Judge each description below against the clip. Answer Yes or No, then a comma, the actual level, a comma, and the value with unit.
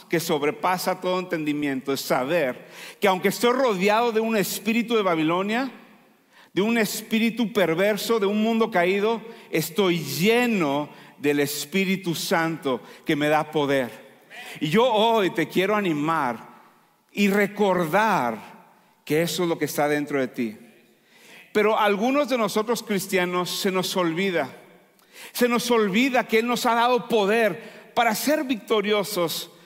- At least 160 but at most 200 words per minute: No, average, 140 wpm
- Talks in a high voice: Yes, high, 195 Hz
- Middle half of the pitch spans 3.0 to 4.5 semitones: No, average, 5.3 semitones